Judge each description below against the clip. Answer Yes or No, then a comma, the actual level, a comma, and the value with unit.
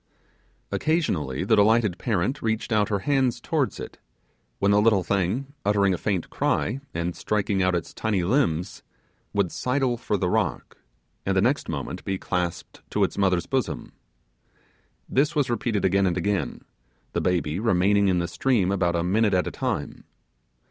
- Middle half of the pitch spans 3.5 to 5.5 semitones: Yes, average, 4.0 semitones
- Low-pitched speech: Yes, low, 100 Hz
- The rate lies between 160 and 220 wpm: Yes, average, 165 wpm